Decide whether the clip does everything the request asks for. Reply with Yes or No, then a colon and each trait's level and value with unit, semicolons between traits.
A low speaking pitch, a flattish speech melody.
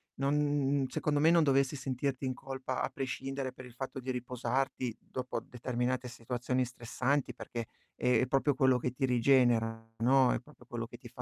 Yes: low, 130 Hz; narrow, 1.8 semitones